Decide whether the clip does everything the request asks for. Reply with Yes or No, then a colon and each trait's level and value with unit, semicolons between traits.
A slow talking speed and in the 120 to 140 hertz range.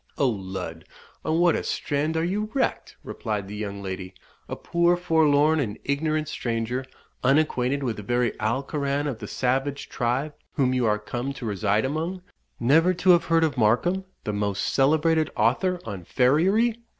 No: average, 165 wpm; low, 135 Hz